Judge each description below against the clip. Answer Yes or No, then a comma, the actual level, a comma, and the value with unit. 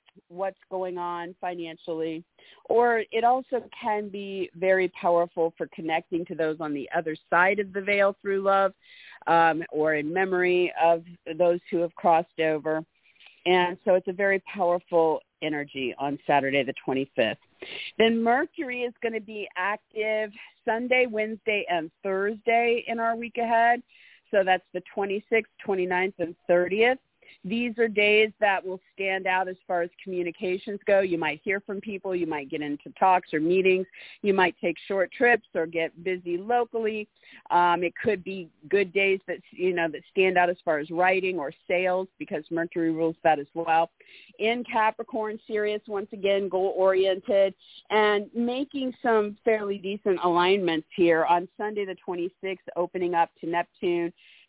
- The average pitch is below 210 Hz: Yes, medium, 185 Hz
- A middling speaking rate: Yes, average, 160 wpm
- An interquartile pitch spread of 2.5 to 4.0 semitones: Yes, average, 3.6 semitones